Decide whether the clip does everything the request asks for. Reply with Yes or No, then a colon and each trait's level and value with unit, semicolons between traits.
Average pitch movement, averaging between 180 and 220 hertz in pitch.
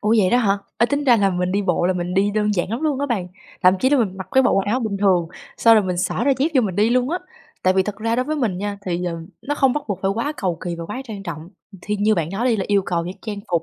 Yes: average, 4.5 semitones; high, 205 Hz